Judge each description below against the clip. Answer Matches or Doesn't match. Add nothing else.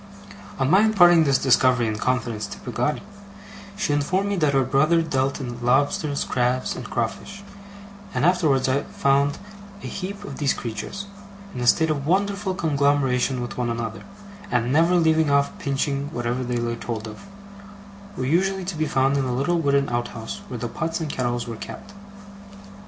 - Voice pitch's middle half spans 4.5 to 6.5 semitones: Matches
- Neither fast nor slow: Matches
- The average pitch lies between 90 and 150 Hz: Matches